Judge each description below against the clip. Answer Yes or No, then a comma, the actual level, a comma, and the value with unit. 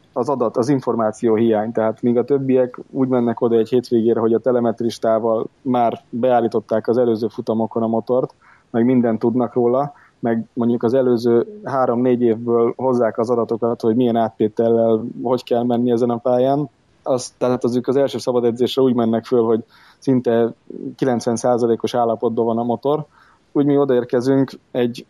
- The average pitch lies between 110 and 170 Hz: Yes, low, 120 Hz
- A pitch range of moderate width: No, narrow, 1.5 semitones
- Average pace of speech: No, fast, 165 wpm